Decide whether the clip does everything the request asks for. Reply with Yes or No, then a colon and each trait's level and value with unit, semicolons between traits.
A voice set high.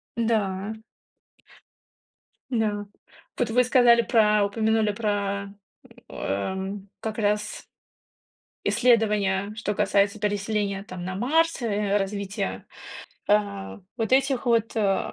Yes: high, 210 Hz